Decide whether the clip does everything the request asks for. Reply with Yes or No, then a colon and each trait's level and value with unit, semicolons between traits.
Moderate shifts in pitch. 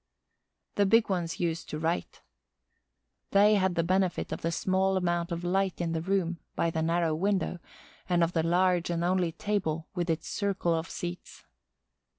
No: narrow, 2.2 semitones